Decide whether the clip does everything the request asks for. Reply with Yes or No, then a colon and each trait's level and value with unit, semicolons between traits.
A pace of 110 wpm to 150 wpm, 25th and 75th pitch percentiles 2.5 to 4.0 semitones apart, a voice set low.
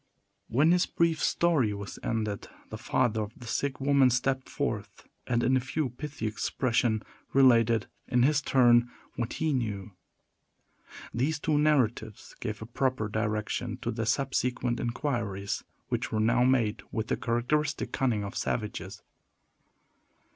Yes: average, 140 wpm; average, 3.7 semitones; low, 120 Hz